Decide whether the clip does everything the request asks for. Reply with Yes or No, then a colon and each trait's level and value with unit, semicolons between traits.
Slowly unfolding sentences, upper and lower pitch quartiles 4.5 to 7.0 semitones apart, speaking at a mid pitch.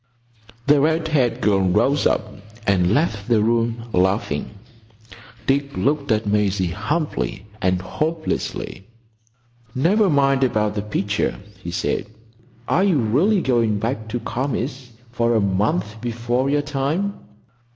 No: slow, 130 wpm; average, 5.3 semitones; low, 120 Hz